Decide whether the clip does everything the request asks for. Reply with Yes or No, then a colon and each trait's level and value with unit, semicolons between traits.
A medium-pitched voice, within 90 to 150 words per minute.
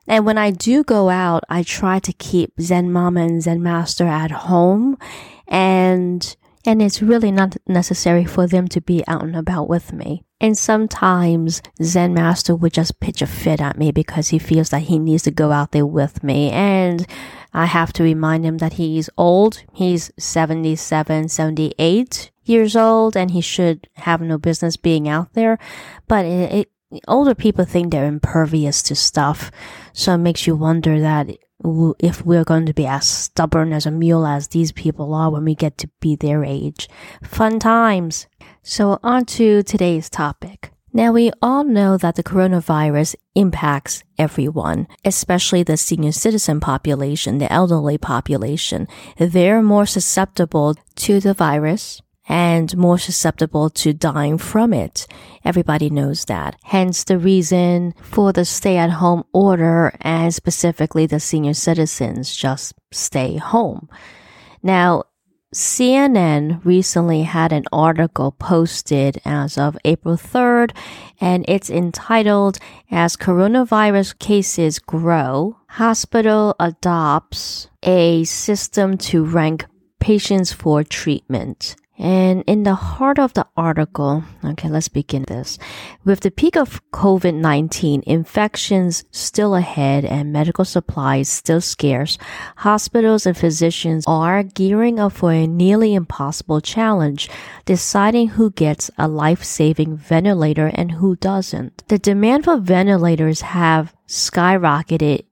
Yes: medium, 170 Hz; average, 140 wpm